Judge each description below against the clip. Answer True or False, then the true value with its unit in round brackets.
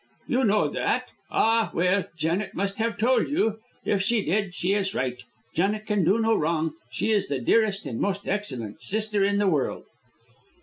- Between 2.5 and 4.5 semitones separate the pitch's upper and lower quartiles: True (3.9 semitones)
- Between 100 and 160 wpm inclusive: False (180 wpm)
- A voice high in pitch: True (200 Hz)